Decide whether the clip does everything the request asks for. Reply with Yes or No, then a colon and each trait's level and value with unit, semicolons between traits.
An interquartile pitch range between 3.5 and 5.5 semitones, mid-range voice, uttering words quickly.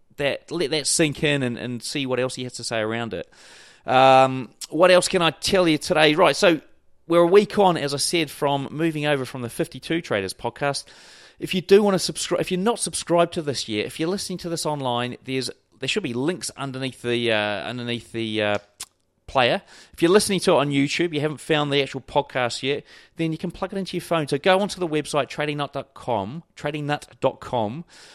Yes: average, 5.0 semitones; medium, 145 Hz; fast, 215 wpm